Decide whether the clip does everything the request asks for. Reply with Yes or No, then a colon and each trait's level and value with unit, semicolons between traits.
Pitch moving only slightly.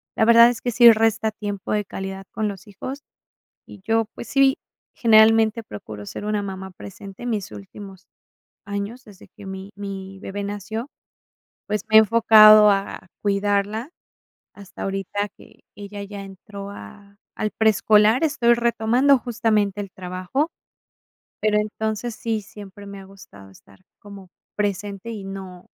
Yes: narrow, 2.2 semitones